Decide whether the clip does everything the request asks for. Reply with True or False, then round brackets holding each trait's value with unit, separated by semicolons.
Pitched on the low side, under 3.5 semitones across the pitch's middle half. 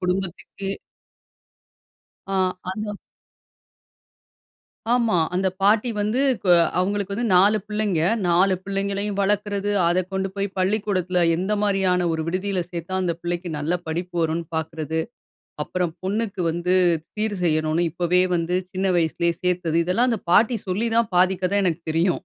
False (185 Hz; 2.8 semitones)